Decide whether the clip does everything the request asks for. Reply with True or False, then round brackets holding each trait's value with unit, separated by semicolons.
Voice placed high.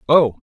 False (135 Hz)